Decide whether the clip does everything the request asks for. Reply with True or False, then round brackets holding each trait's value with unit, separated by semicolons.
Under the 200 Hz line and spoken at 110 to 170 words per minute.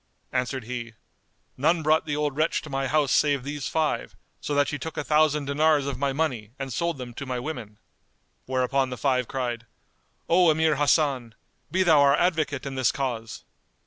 False (140 Hz; 185 wpm)